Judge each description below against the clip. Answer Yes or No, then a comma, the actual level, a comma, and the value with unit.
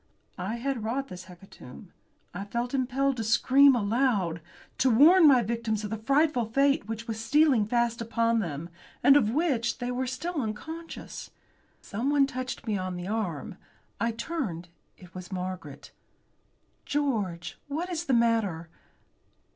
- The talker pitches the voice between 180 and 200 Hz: No, high, 230 Hz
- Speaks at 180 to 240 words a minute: No, average, 145 wpm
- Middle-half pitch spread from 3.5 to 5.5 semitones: Yes, average, 5.2 semitones